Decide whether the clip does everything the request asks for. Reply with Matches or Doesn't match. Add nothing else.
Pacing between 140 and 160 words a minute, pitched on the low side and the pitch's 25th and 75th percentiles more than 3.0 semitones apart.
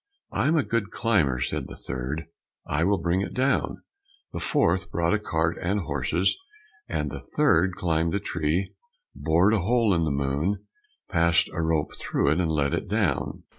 Doesn't match